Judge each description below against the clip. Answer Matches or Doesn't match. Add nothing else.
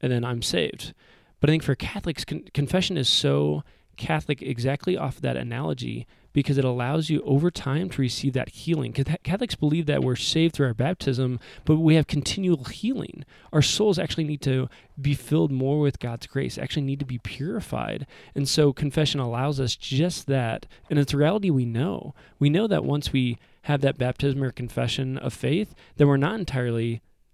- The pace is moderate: Matches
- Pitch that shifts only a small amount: Doesn't match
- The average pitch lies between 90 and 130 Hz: Doesn't match